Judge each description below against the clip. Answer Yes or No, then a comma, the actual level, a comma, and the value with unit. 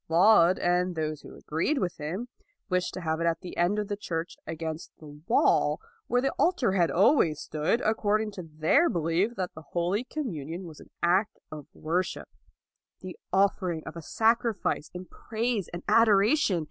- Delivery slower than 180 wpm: No, average, 185 wpm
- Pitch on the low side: No, medium, 180 Hz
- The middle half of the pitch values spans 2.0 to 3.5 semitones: No, average, 4.6 semitones